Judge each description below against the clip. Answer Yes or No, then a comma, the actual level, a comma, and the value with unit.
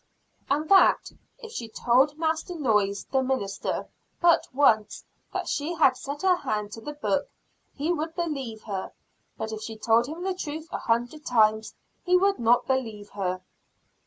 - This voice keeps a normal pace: Yes, average, 165 wpm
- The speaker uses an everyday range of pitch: No, wide, 6.3 semitones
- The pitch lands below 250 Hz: No, very high, 265 Hz